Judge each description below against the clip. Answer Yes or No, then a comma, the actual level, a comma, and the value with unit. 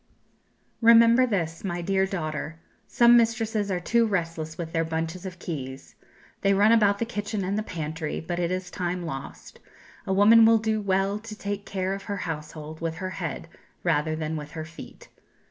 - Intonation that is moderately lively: Yes, average, 4.1 semitones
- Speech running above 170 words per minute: Yes, average, 180 wpm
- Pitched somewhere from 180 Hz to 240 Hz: Yes, medium, 185 Hz